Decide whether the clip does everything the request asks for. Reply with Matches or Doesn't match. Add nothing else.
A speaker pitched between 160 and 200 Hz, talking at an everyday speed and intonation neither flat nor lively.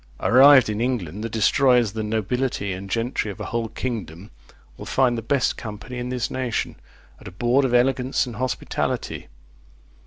Doesn't match